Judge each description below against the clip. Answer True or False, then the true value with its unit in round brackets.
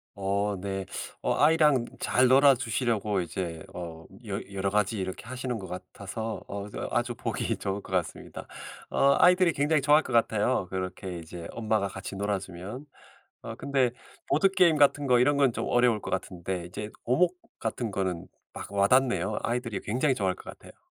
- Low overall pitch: True (105 Hz)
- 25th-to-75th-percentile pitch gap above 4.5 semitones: True (5.3 semitones)